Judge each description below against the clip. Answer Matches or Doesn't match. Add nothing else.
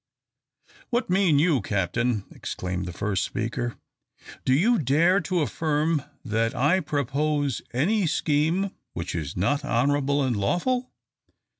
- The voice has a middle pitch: Matches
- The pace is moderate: Doesn't match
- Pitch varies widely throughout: Matches